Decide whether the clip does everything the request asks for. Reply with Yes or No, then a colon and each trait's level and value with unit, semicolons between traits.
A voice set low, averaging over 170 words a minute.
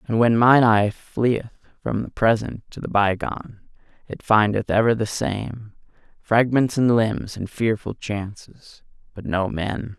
No: low, 110 Hz; average, 145 wpm